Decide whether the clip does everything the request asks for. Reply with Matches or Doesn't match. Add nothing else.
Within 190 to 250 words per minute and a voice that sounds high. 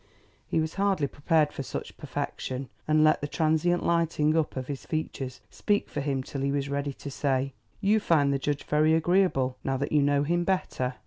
Doesn't match